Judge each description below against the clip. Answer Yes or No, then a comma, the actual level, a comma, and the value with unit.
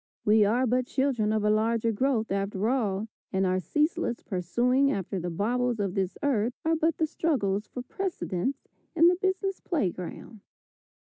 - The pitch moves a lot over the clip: Yes, wide, 5.9 semitones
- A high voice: Yes, high, 230 Hz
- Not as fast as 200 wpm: Yes, average, 170 wpm